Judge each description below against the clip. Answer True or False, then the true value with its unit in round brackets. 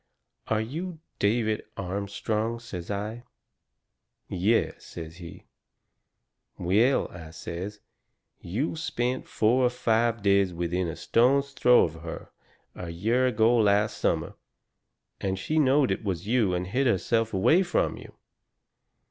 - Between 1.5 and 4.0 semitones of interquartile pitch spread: False (4.8 semitones)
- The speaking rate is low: True (130 wpm)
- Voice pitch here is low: True (110 Hz)